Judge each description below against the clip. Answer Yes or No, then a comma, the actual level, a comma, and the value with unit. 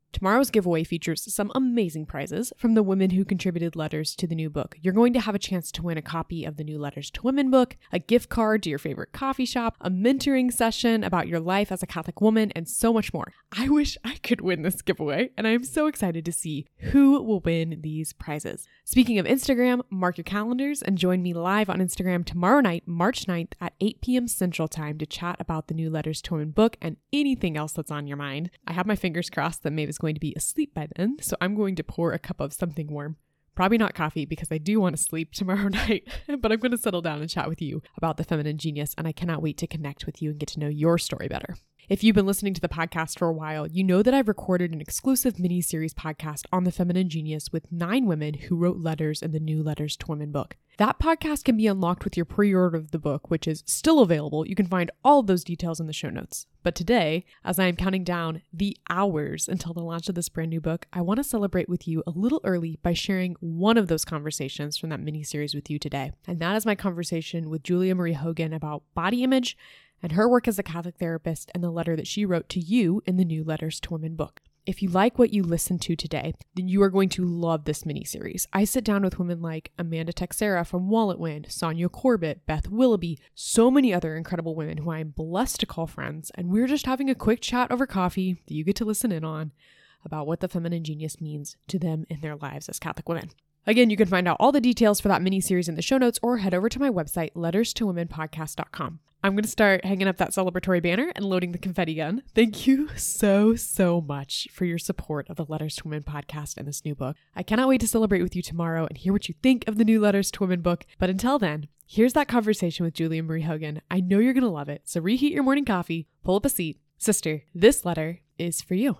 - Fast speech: Yes, fast, 250 wpm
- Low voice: No, medium, 175 Hz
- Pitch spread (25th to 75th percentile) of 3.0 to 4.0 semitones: No, average, 4.8 semitones